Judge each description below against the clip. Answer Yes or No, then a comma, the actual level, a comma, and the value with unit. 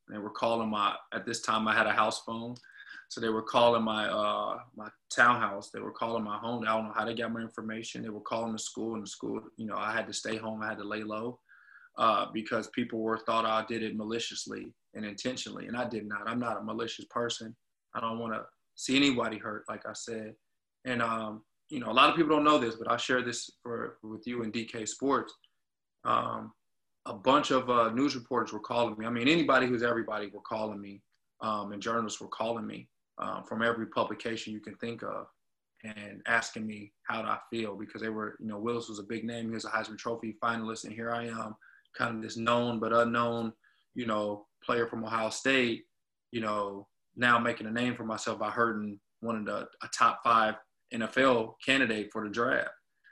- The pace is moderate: No, fast, 220 wpm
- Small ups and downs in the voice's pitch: Yes, narrow, 1.5 semitones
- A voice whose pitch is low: Yes, low, 115 Hz